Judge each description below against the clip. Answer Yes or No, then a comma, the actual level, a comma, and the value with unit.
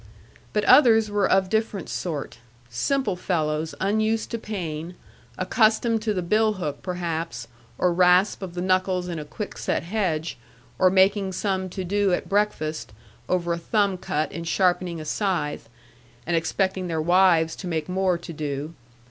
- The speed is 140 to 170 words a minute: Yes, average, 160 wpm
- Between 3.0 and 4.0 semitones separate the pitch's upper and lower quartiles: Yes, average, 3.4 semitones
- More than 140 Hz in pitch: Yes, medium, 185 Hz